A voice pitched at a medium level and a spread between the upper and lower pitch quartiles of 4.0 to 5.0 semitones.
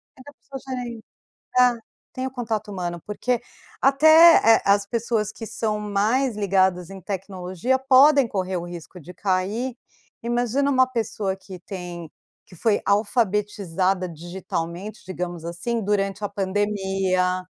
No: high, 205 Hz; average, 4.3 semitones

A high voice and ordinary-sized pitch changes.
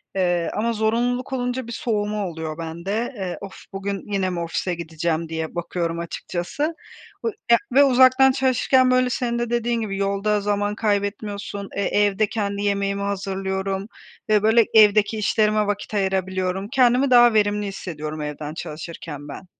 Yes: high, 200 Hz; average, 3.7 semitones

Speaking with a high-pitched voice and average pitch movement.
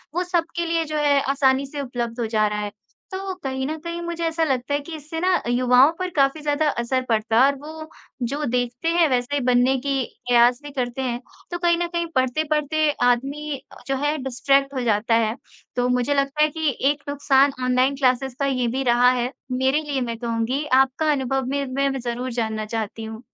Yes: very high, 270 Hz; average, 3.5 semitones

